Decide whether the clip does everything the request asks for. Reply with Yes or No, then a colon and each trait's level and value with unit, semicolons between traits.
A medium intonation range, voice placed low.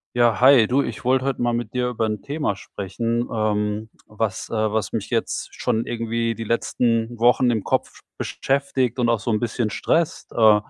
No: narrow, 2.2 semitones; low, 115 Hz